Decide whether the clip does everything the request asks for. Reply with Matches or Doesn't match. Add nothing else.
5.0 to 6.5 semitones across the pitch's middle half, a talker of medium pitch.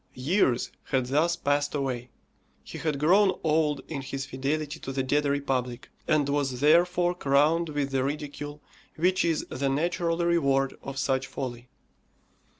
Doesn't match